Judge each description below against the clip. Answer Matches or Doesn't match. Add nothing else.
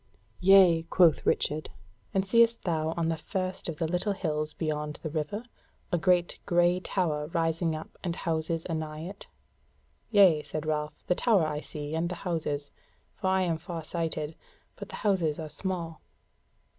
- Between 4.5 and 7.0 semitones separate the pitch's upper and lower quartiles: Doesn't match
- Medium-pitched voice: Matches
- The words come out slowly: Doesn't match